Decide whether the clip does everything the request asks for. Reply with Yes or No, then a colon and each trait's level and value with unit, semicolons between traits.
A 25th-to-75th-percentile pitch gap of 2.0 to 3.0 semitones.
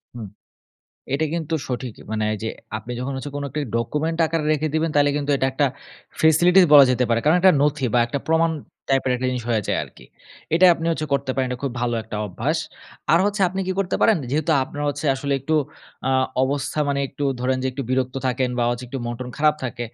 No: average, 3.9 semitones